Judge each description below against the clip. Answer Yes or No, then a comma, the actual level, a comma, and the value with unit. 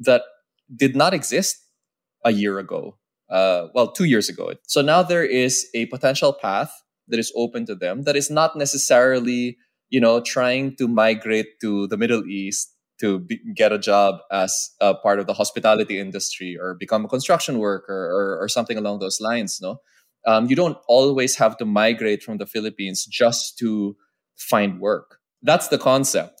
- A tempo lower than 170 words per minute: No, average, 180 wpm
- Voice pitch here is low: Yes, low, 115 Hz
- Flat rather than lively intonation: No, average, 4.4 semitones